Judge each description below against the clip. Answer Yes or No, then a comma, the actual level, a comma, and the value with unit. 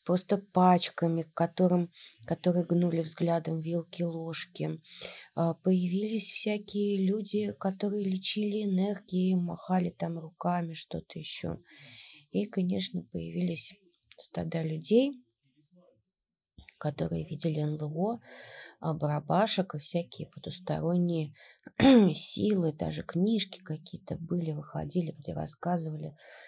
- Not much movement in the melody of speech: No, average, 3.3 semitones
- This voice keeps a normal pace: No, slow, 85 wpm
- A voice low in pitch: No, medium, 175 Hz